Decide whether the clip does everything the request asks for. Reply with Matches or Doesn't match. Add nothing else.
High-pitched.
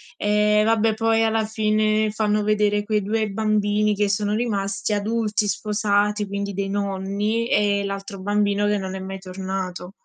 Matches